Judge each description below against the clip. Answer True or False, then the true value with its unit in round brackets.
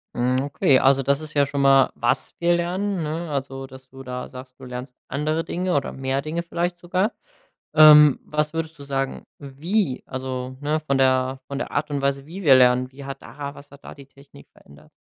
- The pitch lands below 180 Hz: True (140 Hz)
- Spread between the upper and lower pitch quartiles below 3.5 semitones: True (2.8 semitones)